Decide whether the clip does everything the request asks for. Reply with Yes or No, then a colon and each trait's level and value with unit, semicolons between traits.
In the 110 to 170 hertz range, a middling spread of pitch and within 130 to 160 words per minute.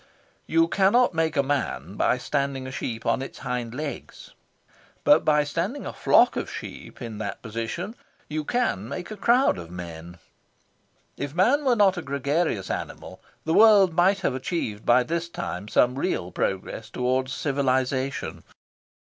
No: medium, 140 Hz; wide, 6.6 semitones; average, 155 wpm